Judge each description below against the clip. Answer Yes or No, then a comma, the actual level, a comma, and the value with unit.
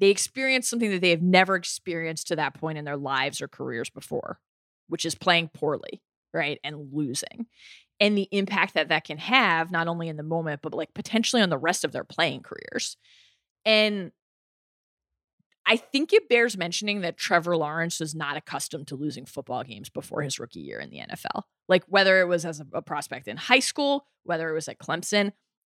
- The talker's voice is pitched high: No, medium, 170 Hz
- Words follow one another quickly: No, average, 195 wpm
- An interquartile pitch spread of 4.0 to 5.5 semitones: Yes, average, 5.0 semitones